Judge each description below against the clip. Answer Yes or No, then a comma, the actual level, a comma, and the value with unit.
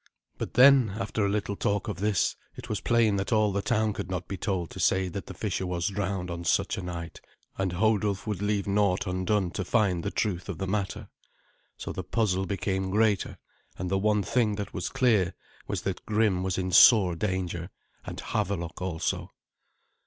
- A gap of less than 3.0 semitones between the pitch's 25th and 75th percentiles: Yes, narrow, 2.5 semitones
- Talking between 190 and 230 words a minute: Yes, average, 195 wpm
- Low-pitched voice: Yes, low, 100 Hz